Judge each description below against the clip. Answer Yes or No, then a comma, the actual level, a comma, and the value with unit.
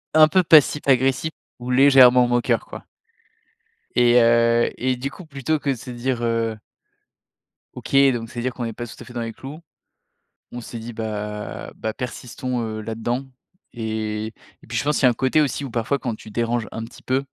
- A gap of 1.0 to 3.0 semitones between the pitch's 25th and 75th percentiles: Yes, narrow, 2.6 semitones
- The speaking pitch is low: Yes, low, 120 Hz